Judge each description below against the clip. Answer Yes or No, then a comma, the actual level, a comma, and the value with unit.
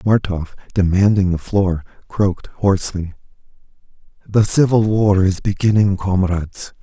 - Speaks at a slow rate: Yes, slow, 105 wpm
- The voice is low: Yes, very low, 95 Hz